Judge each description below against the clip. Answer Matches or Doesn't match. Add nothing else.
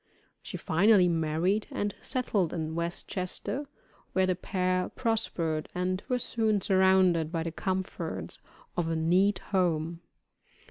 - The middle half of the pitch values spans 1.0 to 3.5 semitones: Matches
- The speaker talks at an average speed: Doesn't match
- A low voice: Doesn't match